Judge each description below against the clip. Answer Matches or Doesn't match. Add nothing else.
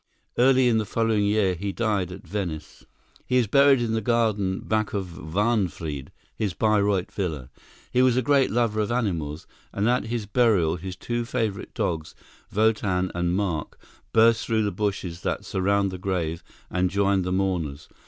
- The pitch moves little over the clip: Doesn't match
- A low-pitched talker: Matches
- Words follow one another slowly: Doesn't match